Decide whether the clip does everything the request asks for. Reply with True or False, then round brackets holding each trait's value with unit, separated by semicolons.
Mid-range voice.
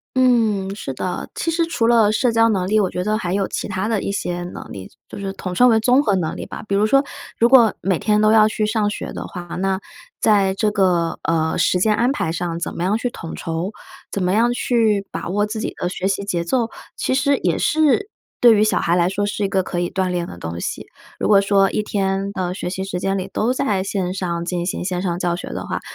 False (195 Hz)